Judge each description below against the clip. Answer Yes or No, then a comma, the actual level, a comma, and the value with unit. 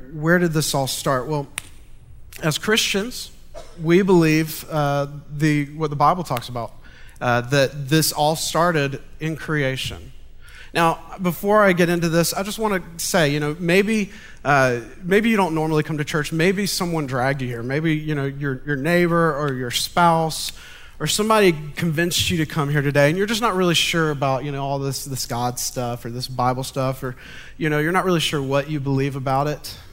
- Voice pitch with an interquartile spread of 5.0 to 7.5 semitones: No, average, 3.9 semitones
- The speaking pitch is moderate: Yes, medium, 150 Hz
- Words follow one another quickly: No, average, 195 wpm